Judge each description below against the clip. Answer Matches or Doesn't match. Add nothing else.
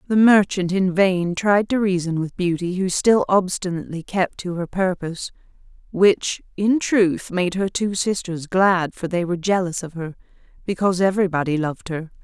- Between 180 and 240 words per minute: Doesn't match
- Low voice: Doesn't match